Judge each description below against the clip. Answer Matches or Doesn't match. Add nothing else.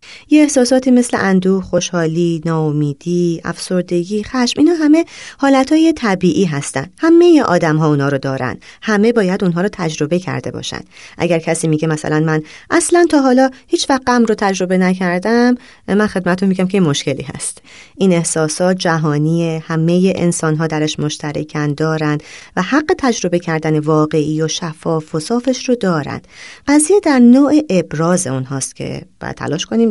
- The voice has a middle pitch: Matches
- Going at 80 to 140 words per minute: Doesn't match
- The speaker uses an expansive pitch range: Matches